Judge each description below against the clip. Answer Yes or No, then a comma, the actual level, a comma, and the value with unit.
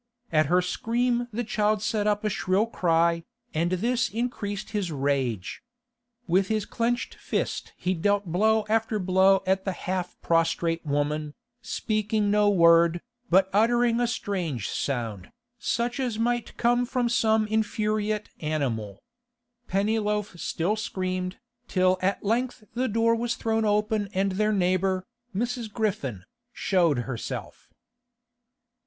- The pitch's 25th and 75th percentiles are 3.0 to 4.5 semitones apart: Yes, average, 4.2 semitones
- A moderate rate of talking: No, slow, 130 wpm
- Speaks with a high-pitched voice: Yes, high, 205 Hz